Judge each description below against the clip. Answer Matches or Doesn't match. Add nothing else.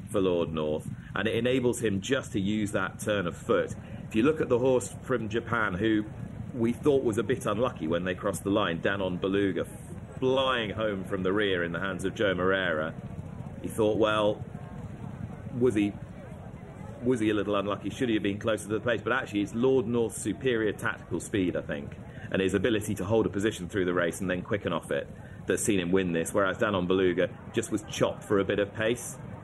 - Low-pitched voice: Matches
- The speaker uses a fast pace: Matches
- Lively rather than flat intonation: Doesn't match